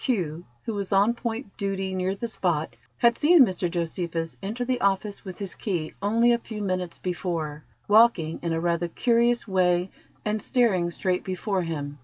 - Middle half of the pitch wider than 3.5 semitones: Yes, average, 4.3 semitones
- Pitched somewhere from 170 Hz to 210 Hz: Yes, high, 190 Hz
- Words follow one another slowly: No, average, 170 wpm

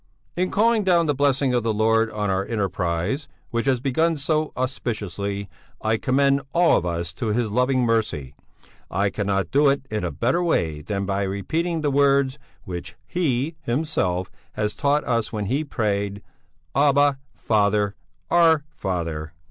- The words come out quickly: No, average, 155 wpm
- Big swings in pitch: Yes, wide, 6.2 semitones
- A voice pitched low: Yes, low, 115 Hz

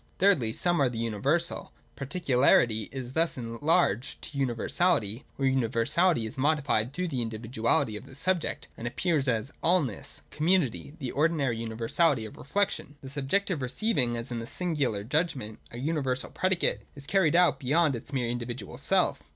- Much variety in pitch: Yes, wide, 5.8 semitones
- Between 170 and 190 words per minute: No, average, 160 wpm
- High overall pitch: No, low, 135 Hz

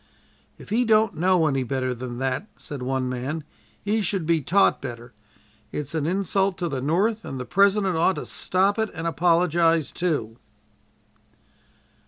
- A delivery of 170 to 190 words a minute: No, average, 160 wpm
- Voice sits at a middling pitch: Yes, medium, 165 Hz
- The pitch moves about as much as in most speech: No, wide, 6.4 semitones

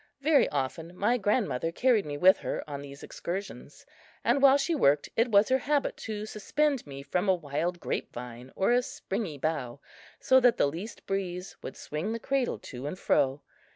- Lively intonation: Yes, wide, 8.7 semitones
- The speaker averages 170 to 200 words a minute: Yes, average, 190 wpm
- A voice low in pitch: No, high, 190 Hz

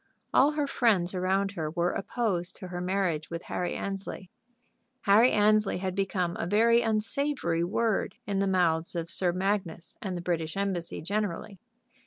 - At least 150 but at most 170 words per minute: Yes, average, 160 wpm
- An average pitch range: Yes, average, 3.2 semitones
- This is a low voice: No, high, 190 Hz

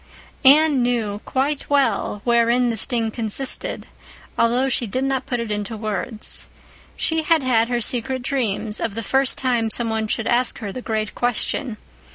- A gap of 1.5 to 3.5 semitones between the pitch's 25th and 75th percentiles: Yes, average, 2.9 semitones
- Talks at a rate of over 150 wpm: Yes, average, 170 wpm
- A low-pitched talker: No, high, 240 Hz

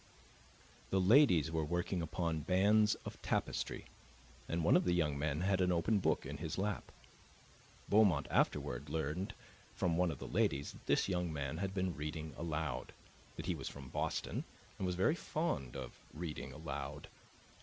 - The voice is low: Yes, very low, 85 Hz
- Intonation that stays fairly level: No, average, 3.8 semitones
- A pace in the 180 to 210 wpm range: No, average, 165 wpm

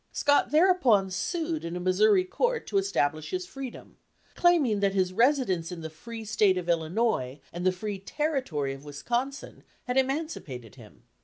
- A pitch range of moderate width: No, wide, 8.2 semitones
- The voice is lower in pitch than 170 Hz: No, high, 210 Hz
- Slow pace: No, average, 160 wpm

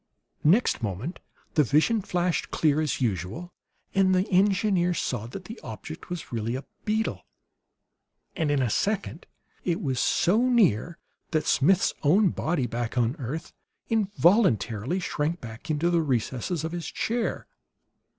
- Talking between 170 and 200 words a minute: No, average, 145 wpm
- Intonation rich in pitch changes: Yes, wide, 6.6 semitones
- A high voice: No, medium, 165 Hz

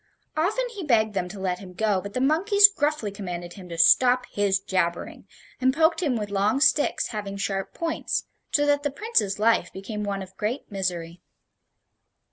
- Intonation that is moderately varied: No, wide, 7.2 semitones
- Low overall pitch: No, high, 210 Hz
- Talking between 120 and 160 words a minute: No, average, 180 wpm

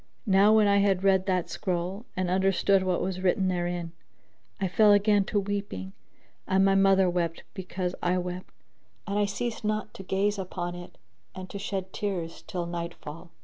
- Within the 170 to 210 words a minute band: Yes, average, 180 wpm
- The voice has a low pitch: No, high, 190 Hz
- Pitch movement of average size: No, narrow, 2.0 semitones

